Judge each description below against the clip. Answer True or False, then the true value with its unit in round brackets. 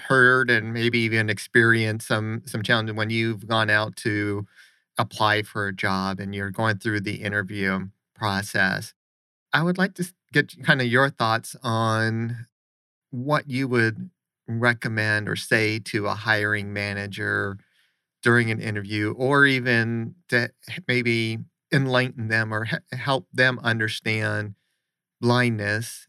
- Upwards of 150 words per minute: False (135 wpm)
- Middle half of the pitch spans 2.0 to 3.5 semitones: True (2.9 semitones)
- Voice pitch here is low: True (110 Hz)